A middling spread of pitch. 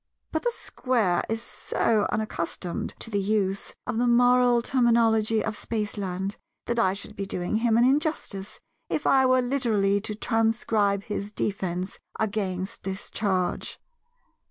Yes: average, 3.3 semitones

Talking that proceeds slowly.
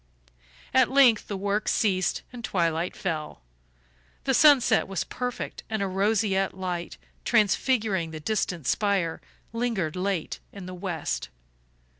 Yes: slow, 125 wpm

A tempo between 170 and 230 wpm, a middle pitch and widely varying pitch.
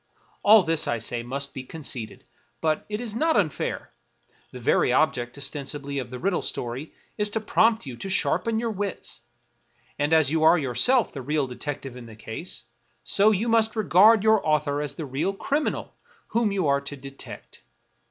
Yes: average, 180 wpm; medium, 155 Hz; wide, 7.6 semitones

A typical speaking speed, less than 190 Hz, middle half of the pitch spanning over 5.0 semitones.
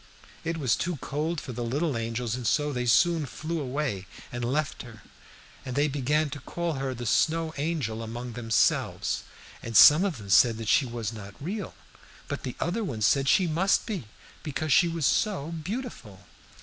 Yes: average, 180 wpm; medium, 140 Hz; wide, 5.6 semitones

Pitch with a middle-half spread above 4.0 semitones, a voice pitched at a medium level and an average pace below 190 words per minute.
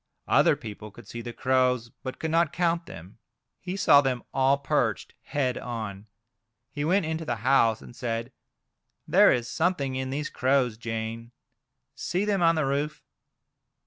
No: average, 4.7 semitones; low, 130 Hz; average, 170 wpm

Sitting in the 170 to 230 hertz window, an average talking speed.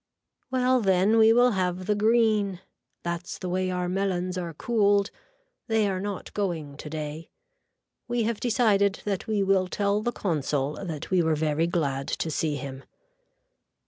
Yes: medium, 185 Hz; average, 155 wpm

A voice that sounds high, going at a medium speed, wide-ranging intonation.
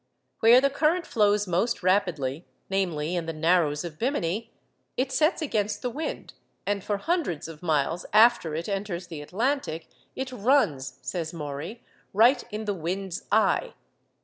Yes: high, 195 Hz; average, 150 wpm; wide, 6.5 semitones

